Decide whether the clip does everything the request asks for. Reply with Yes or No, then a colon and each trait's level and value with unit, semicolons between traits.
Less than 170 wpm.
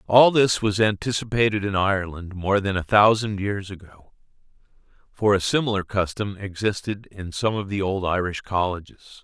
Yes: average, 155 wpm